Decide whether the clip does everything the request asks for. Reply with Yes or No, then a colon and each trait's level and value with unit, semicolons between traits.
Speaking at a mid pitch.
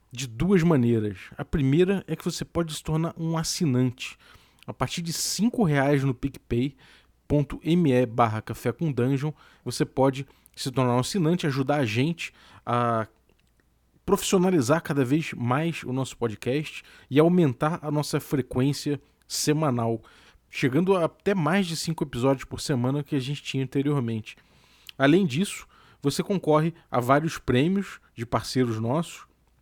Yes: medium, 145 Hz